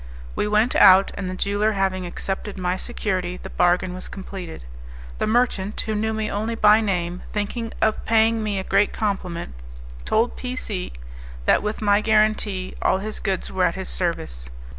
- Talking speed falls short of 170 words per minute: No, average, 175 wpm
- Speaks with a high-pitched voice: Yes, high, 205 Hz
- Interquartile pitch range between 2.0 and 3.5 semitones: Yes, average, 2.7 semitones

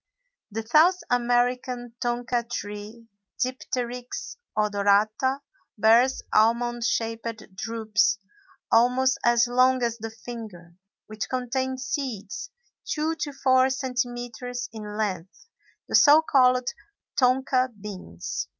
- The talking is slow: Yes, slow, 100 wpm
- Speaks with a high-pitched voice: Yes, high, 240 Hz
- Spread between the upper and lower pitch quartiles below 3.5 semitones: Yes, average, 2.8 semitones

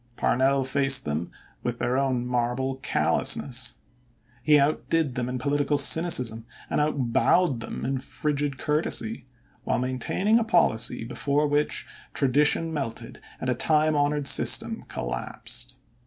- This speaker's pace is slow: Yes, slow, 130 wpm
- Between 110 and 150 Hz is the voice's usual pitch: Yes, low, 135 Hz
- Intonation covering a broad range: No, average, 3.2 semitones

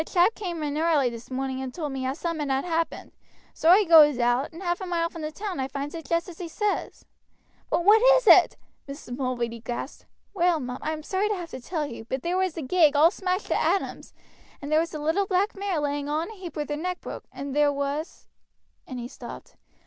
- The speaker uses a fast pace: Yes, fast, 245 wpm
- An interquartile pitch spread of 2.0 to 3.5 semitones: No, average, 4.3 semitones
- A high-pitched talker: Yes, very high, 315 Hz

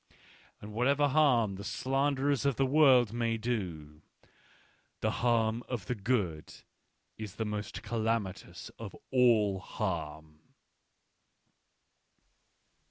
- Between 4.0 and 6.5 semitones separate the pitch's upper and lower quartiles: Yes, average, 4.3 semitones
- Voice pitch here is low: Yes, low, 115 Hz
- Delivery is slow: Yes, slow, 105 wpm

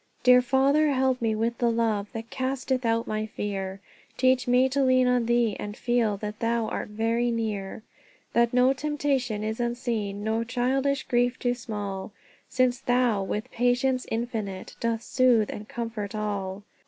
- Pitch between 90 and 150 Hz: No, high, 235 Hz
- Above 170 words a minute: No, average, 160 wpm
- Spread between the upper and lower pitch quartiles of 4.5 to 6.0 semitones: No, average, 2.9 semitones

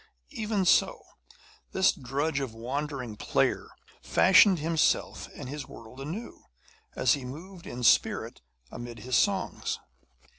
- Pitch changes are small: No, wide, 5.6 semitones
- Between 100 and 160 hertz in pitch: Yes, medium, 140 Hz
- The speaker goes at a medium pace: No, slow, 120 wpm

